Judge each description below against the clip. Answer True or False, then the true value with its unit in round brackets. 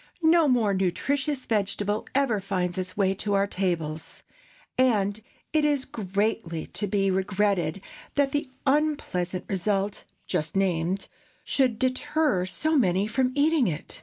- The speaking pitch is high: True (205 Hz)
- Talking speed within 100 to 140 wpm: True (135 wpm)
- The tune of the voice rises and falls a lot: True (6.0 semitones)